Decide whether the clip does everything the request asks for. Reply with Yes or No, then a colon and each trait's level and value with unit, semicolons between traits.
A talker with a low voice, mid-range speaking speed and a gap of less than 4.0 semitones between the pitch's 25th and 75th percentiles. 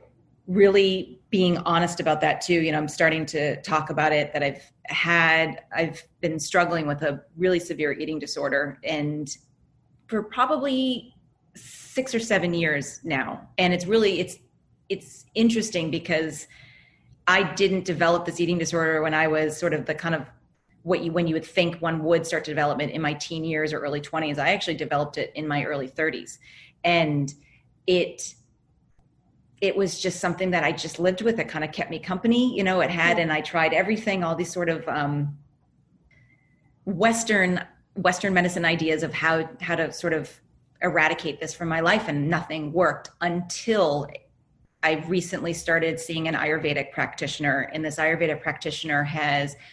No: medium, 160 Hz; average, 170 wpm; average, 2.8 semitones